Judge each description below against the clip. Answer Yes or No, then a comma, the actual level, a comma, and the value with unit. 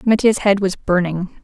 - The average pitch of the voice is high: Yes, high, 195 Hz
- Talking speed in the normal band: Yes, average, 165 wpm